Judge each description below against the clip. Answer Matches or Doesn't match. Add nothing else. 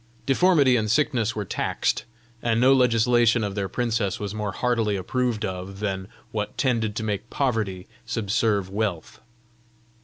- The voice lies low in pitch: Matches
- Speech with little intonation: Doesn't match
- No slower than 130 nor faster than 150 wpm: Matches